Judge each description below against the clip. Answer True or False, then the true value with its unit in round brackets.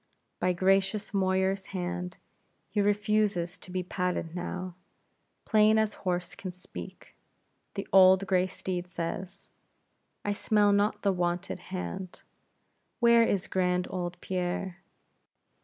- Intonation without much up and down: True (1.9 semitones)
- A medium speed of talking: False (120 wpm)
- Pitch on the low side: False (185 Hz)